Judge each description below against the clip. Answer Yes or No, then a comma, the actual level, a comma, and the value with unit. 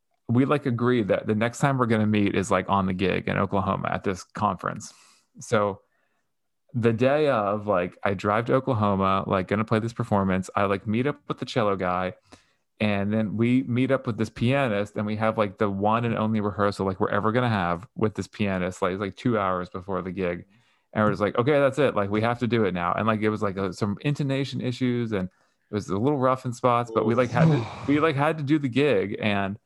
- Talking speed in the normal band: No, fast, 240 wpm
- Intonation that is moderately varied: Yes, average, 3.8 semitones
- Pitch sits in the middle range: No, low, 110 Hz